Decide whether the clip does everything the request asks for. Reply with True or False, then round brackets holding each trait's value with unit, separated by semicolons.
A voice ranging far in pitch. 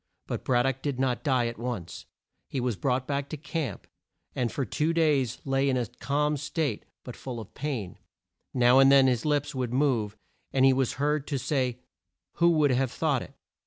False (2.8 semitones)